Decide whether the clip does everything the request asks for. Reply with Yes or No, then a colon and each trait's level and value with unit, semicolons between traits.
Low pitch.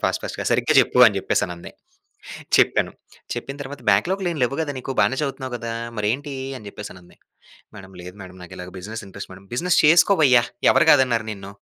Yes: low, 120 Hz